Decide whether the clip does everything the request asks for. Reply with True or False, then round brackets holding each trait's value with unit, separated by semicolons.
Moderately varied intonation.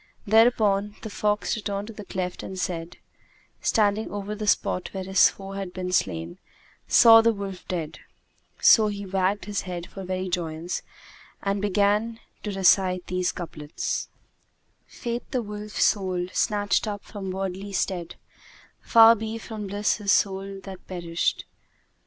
False (2.2 semitones)